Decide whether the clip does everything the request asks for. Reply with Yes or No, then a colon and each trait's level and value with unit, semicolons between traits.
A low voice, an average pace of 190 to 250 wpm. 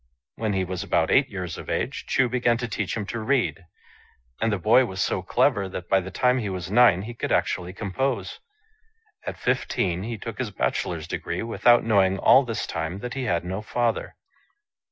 Yes: low, 105 Hz; average, 195 wpm